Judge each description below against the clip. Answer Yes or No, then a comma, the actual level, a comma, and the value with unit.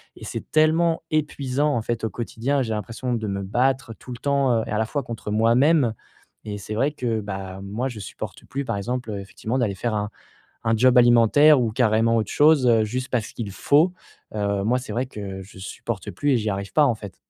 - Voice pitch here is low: Yes, low, 115 Hz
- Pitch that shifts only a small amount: No, average, 3.8 semitones